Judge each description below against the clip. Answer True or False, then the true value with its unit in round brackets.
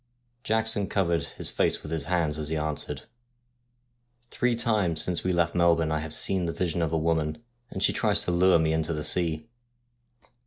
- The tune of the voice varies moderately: True (3.9 semitones)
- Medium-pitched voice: False (85 Hz)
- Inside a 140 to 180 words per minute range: False (195 wpm)